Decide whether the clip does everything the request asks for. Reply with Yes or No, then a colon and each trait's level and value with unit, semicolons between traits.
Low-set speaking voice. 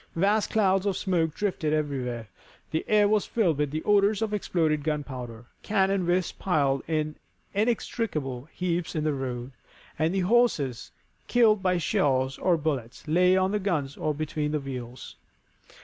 No: medium, 160 Hz